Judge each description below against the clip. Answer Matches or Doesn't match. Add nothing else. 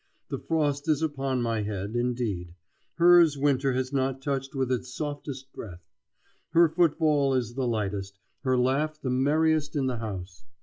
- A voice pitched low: Matches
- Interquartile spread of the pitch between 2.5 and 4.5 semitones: Matches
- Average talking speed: Matches